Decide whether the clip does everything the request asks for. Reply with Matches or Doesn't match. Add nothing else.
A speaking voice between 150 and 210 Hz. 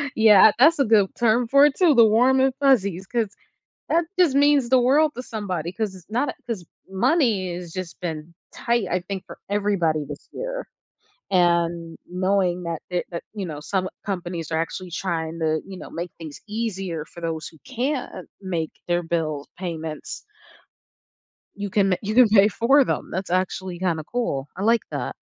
Matches